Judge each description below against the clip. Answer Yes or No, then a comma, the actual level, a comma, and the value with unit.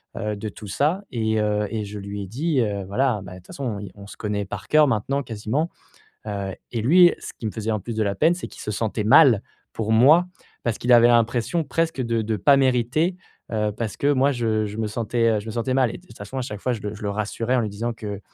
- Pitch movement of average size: Yes, average, 3.7 semitones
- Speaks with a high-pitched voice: No, low, 110 Hz